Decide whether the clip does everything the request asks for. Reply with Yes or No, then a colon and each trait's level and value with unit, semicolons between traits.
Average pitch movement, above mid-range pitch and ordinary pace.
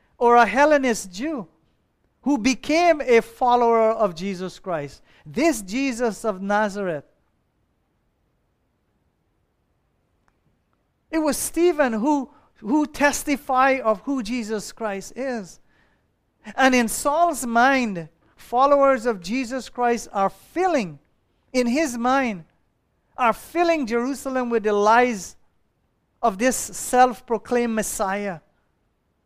No: average, 4.3 semitones; high, 240 Hz; slow, 100 wpm